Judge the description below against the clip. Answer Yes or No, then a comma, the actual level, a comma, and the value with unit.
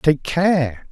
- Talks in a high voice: No, medium, 155 Hz